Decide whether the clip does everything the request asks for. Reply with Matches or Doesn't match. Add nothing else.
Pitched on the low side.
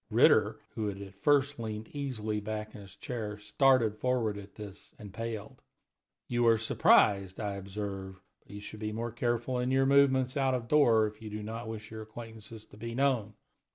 Matches